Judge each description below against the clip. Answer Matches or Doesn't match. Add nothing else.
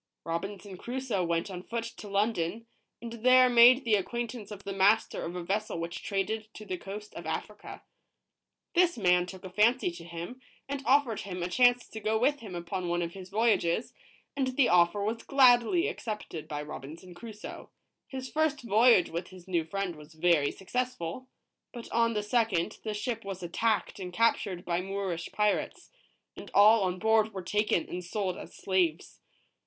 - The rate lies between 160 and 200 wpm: Matches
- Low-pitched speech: Doesn't match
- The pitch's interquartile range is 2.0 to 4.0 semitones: Doesn't match